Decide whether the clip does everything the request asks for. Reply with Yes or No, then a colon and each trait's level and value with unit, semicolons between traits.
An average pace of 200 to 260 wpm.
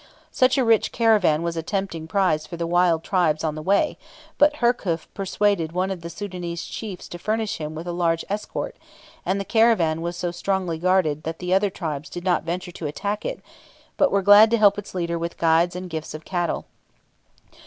Yes: fast, 205 wpm